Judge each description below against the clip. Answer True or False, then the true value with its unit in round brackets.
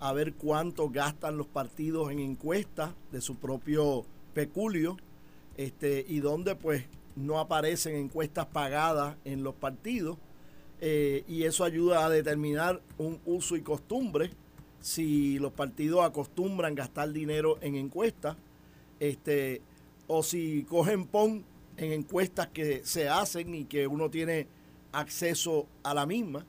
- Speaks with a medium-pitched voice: True (155 Hz)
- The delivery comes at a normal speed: True (135 wpm)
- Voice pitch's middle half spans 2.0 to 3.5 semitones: True (2.6 semitones)